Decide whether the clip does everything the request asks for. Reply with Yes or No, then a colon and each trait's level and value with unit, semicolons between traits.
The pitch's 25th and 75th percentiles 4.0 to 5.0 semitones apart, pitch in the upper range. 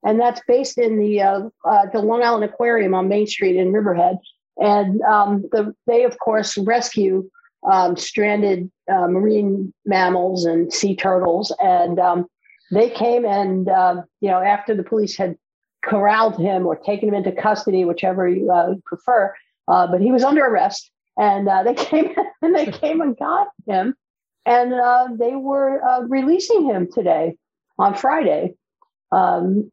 Yes: average, 4.3 semitones; high, 210 Hz